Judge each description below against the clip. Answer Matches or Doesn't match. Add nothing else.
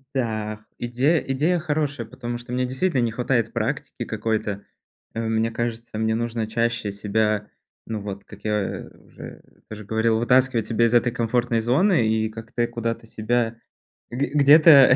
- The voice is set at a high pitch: Doesn't match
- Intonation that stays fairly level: Matches